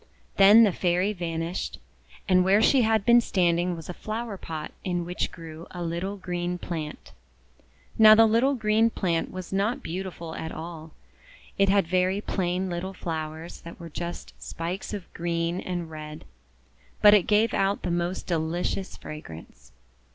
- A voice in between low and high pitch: Yes, medium, 180 Hz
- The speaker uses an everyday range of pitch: Yes, average, 3.0 semitones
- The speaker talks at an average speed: Yes, average, 160 wpm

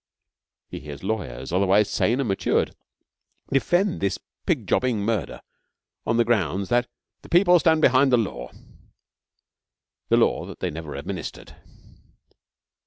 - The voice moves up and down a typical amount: No, wide, 5.8 semitones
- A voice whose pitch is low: Yes, low, 110 Hz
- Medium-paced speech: No, slow, 130 wpm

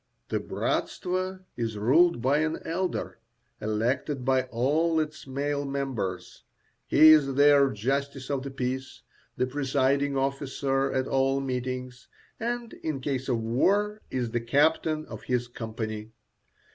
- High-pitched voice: No, low, 135 Hz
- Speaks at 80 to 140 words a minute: Yes, slow, 135 wpm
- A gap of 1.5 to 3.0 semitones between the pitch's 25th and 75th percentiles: Yes, average, 2.7 semitones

